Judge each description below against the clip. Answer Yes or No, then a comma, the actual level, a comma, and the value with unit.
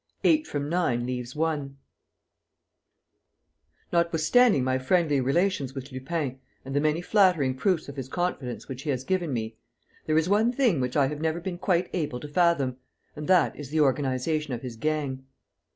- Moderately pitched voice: Yes, medium, 150 Hz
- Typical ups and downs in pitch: Yes, average, 4.6 semitones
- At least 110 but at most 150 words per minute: No, average, 170 wpm